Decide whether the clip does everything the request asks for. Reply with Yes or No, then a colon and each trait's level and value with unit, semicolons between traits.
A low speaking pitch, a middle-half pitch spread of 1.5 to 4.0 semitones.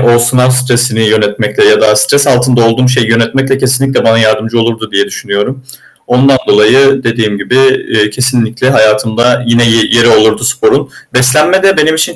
Yes: low, 125 Hz; average, 2.9 semitones